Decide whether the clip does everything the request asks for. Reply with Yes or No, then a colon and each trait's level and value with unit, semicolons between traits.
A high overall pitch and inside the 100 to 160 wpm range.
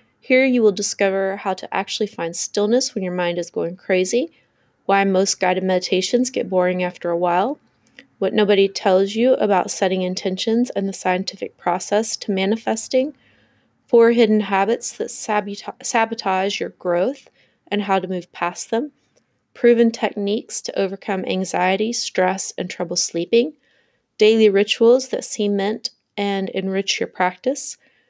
Yes: high, 200 Hz; average, 145 wpm